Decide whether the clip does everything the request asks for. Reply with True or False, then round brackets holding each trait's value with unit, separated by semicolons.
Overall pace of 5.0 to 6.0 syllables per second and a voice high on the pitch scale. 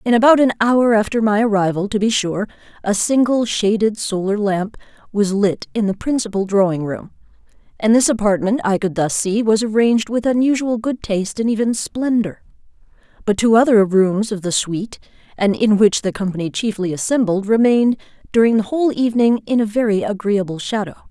True (5.5 syllables/s; 215 Hz)